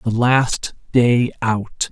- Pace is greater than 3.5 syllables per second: No, 2.6 syllables/s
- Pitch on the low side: Yes, low, 120 Hz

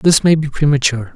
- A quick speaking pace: Yes, fast, 210 wpm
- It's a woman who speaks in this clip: No, male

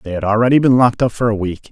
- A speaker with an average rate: No, fast, 315 wpm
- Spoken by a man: Yes, male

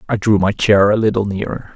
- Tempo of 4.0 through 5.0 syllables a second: No, 5.8 syllables/s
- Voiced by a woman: No, male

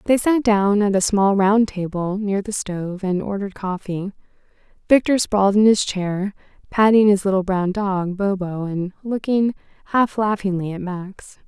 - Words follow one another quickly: No, average, 160 wpm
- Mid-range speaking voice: No, high, 200 Hz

